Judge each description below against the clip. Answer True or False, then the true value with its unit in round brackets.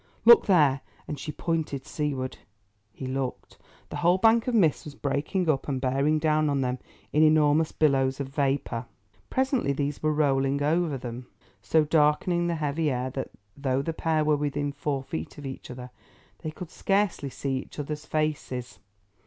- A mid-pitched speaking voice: True (145 Hz)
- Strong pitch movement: False (2.6 semitones)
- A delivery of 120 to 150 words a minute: False (170 wpm)